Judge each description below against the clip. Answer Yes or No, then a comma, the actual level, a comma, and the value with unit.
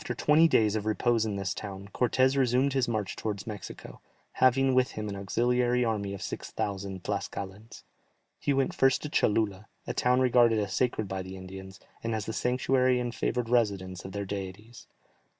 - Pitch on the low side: Yes, low, 110 Hz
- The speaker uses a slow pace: No, average, 185 wpm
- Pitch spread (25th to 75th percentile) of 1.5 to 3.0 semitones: No, average, 4.0 semitones